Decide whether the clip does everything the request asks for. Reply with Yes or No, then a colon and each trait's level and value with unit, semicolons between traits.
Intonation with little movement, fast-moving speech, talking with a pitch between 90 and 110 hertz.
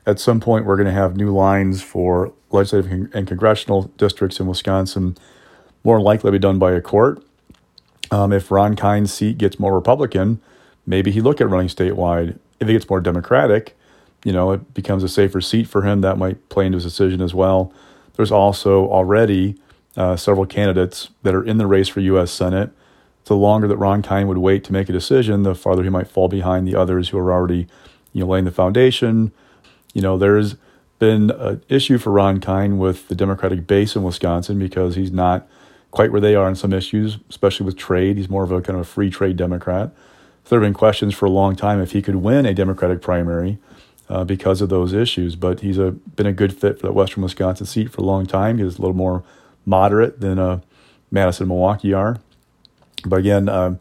Yes: narrow, 1.7 semitones; fast, 215 wpm; very low, 95 Hz